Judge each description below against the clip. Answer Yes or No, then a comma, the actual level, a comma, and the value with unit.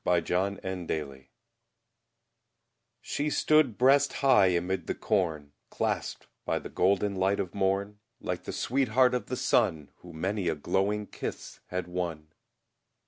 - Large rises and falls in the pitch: No, average, 3.4 semitones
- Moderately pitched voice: No, very low, 95 Hz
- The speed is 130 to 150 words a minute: Yes, average, 140 wpm